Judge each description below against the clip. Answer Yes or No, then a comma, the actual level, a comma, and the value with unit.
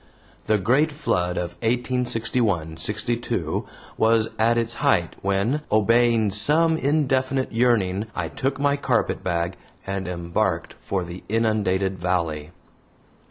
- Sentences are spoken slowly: Yes, slow, 115 wpm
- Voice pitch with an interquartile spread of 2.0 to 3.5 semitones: No, average, 5.2 semitones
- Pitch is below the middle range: Yes, low, 110 Hz